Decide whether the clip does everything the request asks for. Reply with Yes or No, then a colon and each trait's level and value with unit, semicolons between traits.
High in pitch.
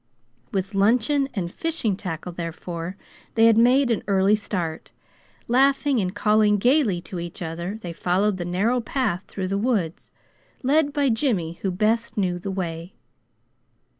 Yes: high, 200 Hz